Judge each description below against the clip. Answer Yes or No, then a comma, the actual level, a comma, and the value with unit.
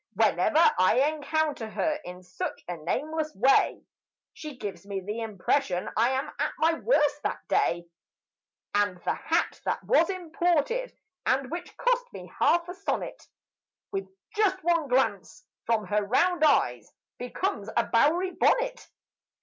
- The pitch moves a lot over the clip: Yes, wide, 8.4 semitones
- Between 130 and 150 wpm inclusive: Yes, average, 140 wpm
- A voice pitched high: Yes, very high, 295 Hz